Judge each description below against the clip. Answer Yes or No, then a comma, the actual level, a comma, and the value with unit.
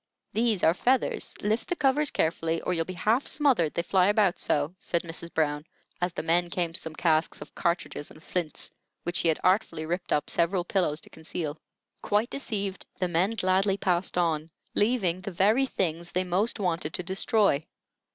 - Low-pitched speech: No, medium, 180 Hz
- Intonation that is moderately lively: Yes, average, 3.5 semitones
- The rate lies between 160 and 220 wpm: Yes, average, 185 wpm